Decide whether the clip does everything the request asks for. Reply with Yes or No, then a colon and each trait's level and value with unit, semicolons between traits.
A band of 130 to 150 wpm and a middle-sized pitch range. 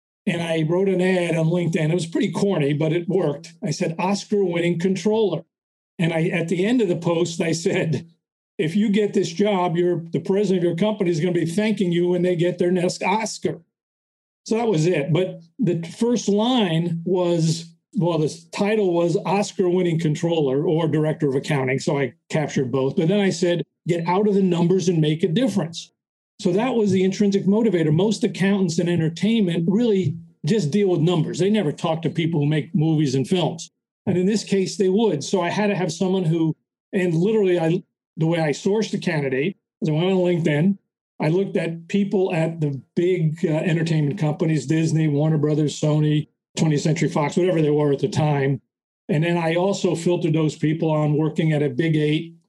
No: average, 200 wpm; average, 3.3 semitones